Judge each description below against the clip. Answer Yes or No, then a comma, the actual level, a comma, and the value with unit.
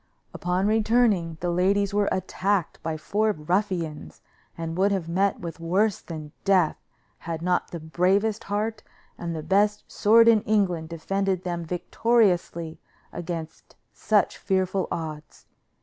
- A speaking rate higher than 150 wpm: No, slow, 135 wpm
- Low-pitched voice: No, medium, 185 Hz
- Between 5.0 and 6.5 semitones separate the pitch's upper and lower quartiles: No, average, 3.5 semitones